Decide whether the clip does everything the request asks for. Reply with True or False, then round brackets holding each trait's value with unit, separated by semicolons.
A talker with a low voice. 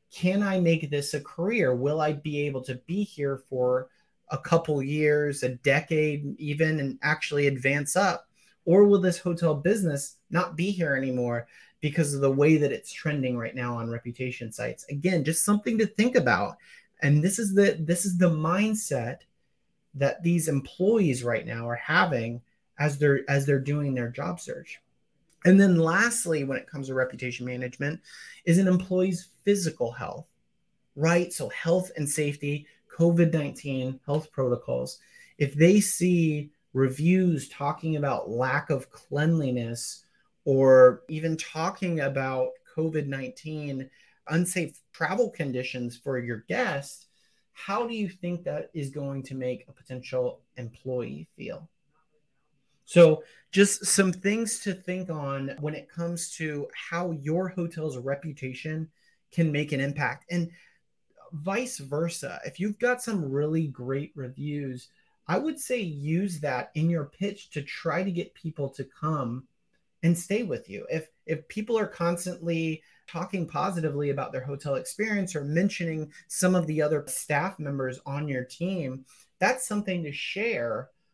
False (155 Hz)